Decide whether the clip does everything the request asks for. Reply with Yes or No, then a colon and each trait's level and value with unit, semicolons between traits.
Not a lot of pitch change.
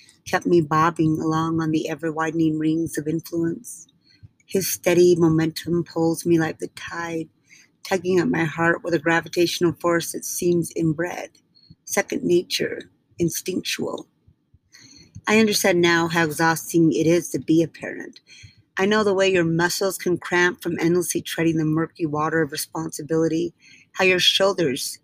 Yes: narrow, 1.6 semitones